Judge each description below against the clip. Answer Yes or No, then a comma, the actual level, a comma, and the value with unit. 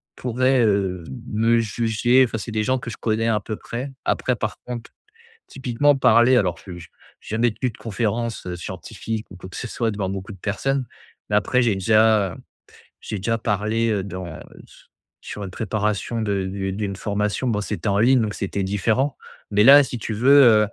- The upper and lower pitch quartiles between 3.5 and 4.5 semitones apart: No, average, 2.9 semitones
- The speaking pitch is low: Yes, low, 110 Hz